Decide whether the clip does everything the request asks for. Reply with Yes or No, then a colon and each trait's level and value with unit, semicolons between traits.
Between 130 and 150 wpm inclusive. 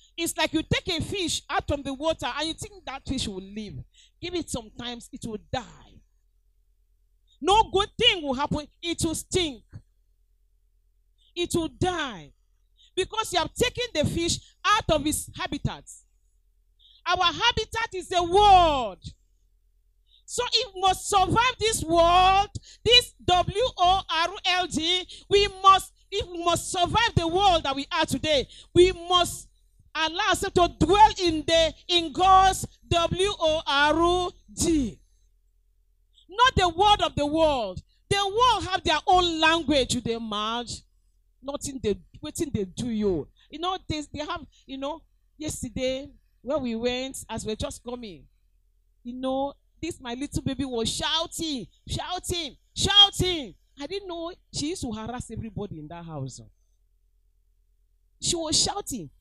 Yes: average, 140 wpm